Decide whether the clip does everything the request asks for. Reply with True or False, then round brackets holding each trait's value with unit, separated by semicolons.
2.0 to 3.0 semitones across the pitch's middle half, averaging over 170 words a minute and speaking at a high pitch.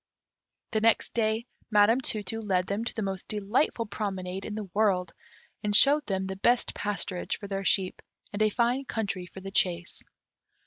True (2.6 semitones; 180 wpm; 205 Hz)